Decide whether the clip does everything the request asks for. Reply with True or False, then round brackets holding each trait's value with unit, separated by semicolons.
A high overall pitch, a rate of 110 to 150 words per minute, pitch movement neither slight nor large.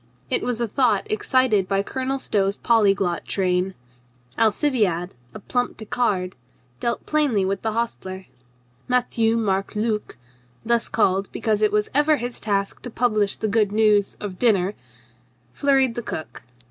True (215 Hz; 145 wpm; 3.5 semitones)